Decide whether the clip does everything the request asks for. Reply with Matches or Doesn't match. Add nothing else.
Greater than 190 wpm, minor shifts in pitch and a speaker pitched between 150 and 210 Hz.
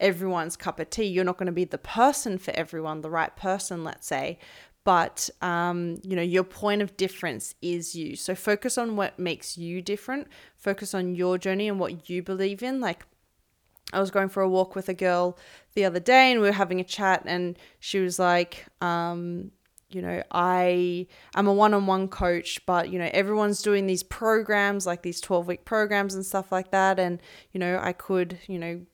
Matches